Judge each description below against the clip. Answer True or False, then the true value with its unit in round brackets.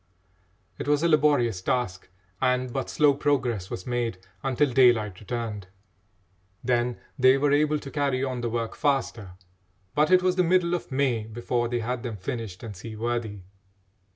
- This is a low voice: True (125 Hz)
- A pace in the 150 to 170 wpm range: True (160 wpm)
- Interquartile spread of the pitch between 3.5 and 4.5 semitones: True (3.9 semitones)